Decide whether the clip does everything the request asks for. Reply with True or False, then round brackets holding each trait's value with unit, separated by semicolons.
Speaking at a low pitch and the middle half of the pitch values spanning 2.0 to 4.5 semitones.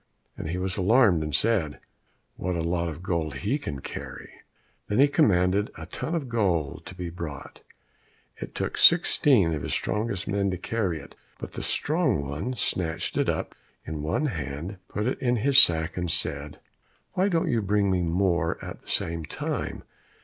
False (90 Hz; 5.6 semitones)